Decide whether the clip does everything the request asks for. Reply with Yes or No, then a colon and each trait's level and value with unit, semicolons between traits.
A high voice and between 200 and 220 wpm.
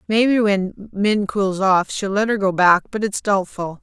Yes: high, 200 Hz; fast, 205 wpm